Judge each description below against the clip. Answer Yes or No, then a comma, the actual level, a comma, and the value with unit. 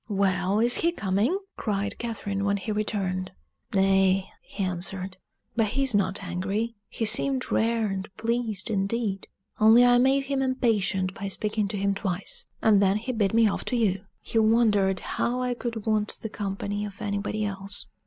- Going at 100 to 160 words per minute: No, average, 175 wpm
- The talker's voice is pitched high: Yes, high, 210 Hz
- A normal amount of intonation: Yes, average, 3.0 semitones